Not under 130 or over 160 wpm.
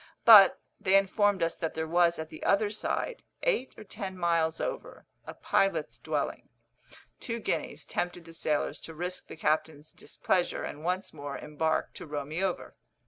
No: average, 170 wpm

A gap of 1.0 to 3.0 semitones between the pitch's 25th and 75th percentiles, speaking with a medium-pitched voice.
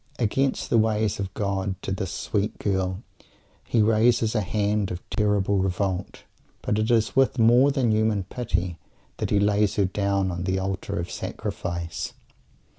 No: narrow, 2.6 semitones; low, 100 Hz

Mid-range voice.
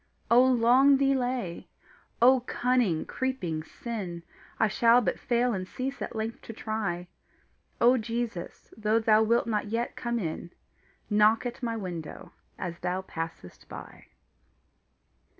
No: high, 225 Hz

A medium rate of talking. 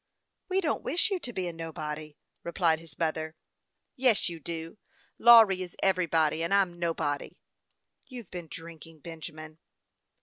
Yes: average, 160 wpm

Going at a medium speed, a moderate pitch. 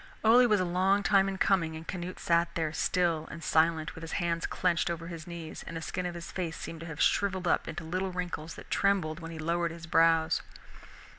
No: fast, 225 wpm; medium, 170 Hz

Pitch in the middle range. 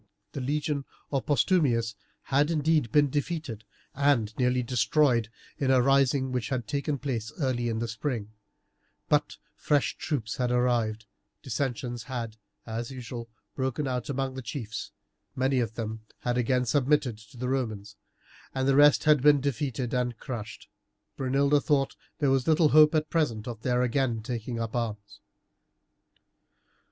No: low, 130 Hz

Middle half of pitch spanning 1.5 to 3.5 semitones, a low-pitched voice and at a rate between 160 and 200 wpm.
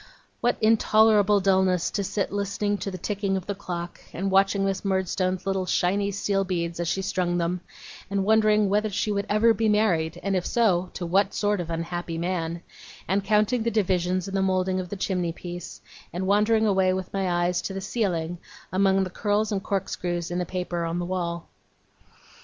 No: narrow, 2.4 semitones; high, 190 Hz; average, 195 wpm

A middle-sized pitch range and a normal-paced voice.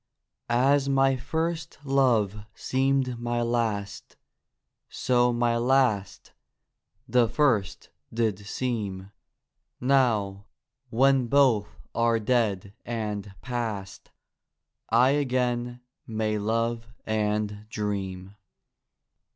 No: average, 3.5 semitones; slow, 85 wpm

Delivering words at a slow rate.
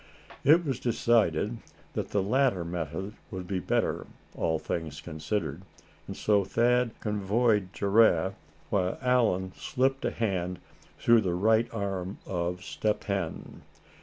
Yes: slow, 130 wpm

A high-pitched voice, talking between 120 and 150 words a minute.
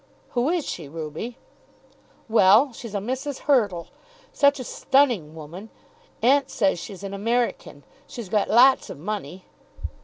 Yes: high, 220 Hz; average, 140 wpm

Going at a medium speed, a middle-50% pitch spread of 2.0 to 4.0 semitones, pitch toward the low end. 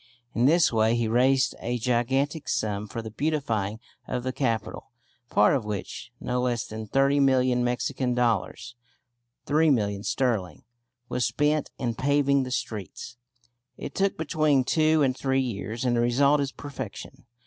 Yes: average, 150 wpm; average, 3.4 semitones; low, 125 Hz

